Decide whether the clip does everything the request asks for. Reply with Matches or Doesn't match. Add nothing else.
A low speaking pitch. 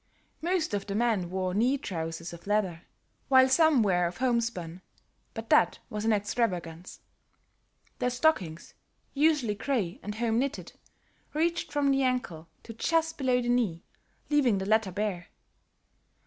Doesn't match